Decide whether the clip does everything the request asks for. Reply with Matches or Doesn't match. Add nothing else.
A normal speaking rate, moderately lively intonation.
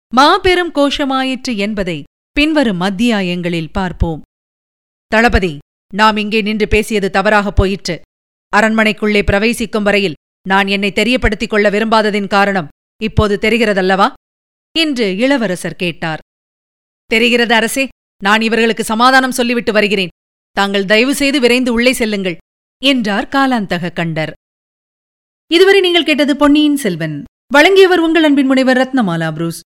Matches